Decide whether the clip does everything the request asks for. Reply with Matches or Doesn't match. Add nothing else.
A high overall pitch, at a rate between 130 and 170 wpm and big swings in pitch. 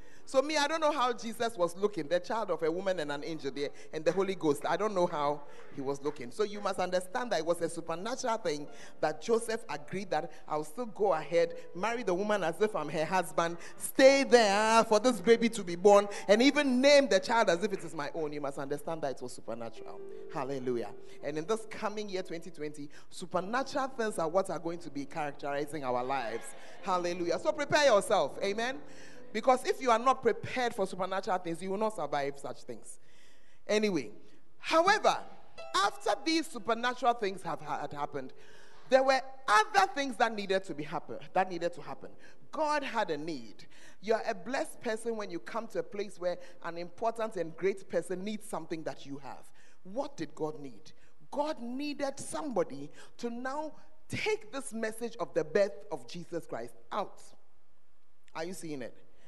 Doesn't match